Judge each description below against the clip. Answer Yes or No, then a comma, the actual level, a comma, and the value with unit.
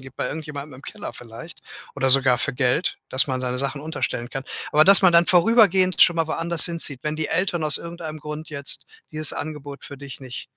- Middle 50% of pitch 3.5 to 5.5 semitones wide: Yes, average, 3.8 semitones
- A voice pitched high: No, medium, 150 Hz